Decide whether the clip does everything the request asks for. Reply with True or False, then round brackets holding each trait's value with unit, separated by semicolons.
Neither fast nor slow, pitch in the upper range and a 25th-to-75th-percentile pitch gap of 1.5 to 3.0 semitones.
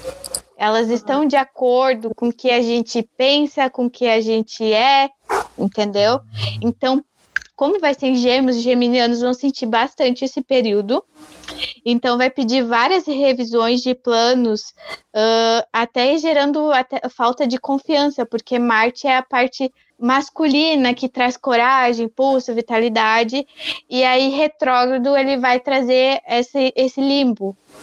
True (140 wpm; 255 Hz; 2.5 semitones)